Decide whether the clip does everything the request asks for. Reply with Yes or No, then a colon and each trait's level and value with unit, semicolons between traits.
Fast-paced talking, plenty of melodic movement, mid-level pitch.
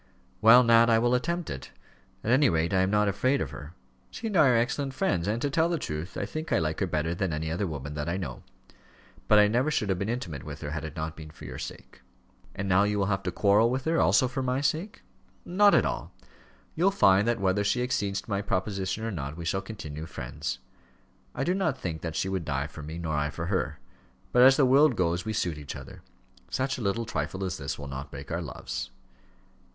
No: fast, 240 wpm; wide, 7.6 semitones; low, 100 Hz